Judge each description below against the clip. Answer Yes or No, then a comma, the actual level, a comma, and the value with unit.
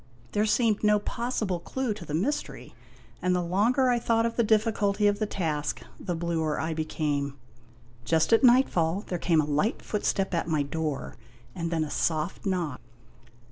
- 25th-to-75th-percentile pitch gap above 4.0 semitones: Yes, average, 5.1 semitones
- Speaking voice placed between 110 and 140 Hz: No, medium, 180 Hz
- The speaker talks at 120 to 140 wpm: No, average, 180 wpm